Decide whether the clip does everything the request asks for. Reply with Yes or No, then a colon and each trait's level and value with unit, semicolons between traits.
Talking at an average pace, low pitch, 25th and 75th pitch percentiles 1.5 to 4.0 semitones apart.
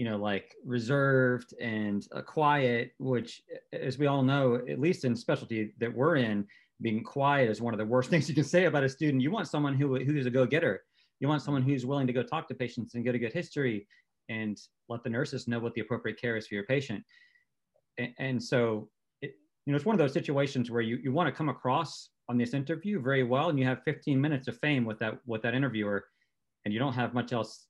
No: fast, 235 wpm; low, 130 Hz; average, 3.5 semitones